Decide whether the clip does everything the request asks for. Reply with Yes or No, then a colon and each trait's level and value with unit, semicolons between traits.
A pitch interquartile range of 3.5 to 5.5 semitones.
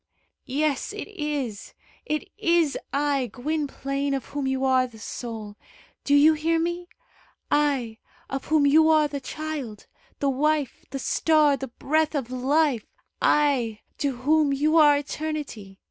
No: average, 2.9 semitones